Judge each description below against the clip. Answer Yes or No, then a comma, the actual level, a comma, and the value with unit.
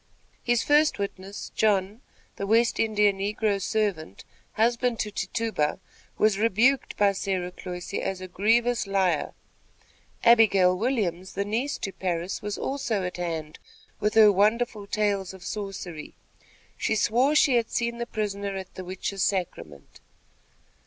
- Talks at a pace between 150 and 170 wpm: No, average, 140 wpm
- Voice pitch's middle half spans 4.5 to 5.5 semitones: No, average, 3.2 semitones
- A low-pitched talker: No, high, 205 Hz